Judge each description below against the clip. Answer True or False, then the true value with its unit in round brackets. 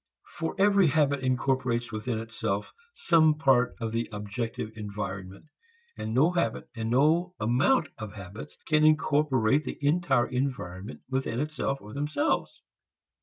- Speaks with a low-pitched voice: True (130 Hz)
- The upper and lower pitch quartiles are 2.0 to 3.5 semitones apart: False (5.6 semitones)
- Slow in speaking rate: True (130 wpm)